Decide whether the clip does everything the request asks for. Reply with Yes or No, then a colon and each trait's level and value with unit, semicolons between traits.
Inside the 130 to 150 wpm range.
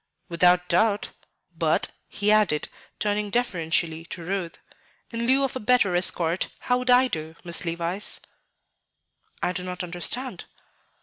Yes: slow, 135 wpm